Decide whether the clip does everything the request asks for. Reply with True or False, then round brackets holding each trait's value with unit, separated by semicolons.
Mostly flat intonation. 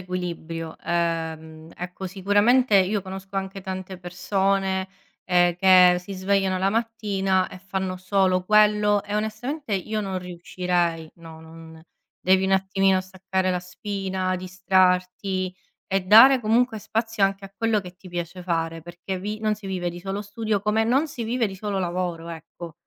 True (2.3 semitones)